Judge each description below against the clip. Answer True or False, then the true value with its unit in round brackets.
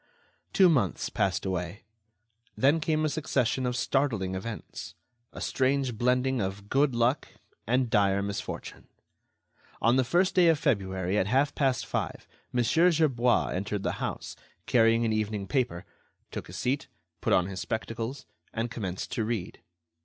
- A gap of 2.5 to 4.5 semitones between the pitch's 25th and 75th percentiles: False (5.1 semitones)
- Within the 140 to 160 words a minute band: True (150 wpm)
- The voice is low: True (120 Hz)